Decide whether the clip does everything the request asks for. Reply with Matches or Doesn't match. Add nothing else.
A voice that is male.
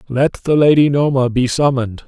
Matches